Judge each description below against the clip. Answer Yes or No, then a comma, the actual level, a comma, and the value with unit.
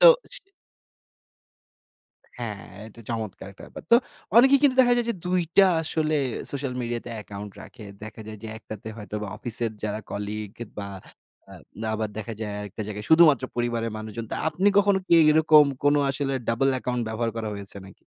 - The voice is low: Yes, low, 115 Hz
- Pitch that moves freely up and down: Yes, wide, 5.9 semitones